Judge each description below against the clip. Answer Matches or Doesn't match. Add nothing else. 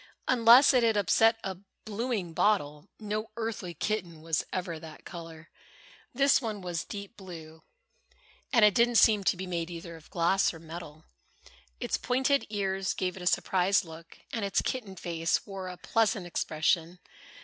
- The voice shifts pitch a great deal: Doesn't match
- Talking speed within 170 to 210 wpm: Doesn't match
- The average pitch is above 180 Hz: Matches